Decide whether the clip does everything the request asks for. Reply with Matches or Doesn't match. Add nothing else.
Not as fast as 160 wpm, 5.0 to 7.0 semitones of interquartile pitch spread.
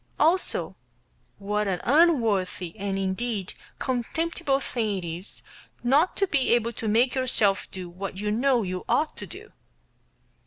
Matches